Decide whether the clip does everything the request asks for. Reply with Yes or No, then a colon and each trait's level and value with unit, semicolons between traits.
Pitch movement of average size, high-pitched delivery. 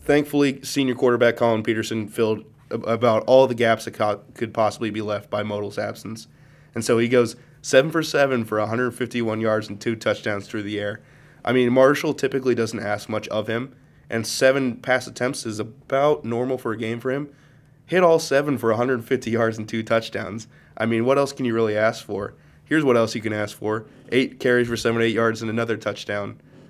No: average, 3.1 semitones; low, 115 Hz